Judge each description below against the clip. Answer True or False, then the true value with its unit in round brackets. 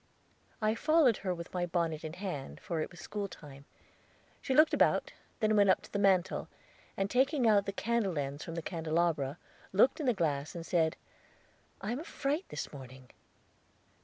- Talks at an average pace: True (185 wpm)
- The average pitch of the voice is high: False (180 Hz)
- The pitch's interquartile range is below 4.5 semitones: False (5.4 semitones)